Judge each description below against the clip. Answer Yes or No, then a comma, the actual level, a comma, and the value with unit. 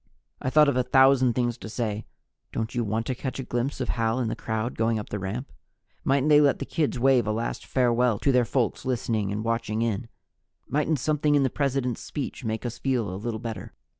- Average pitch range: Yes, average, 3.0 semitones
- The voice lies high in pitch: No, low, 120 Hz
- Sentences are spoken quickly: Yes, fast, 225 wpm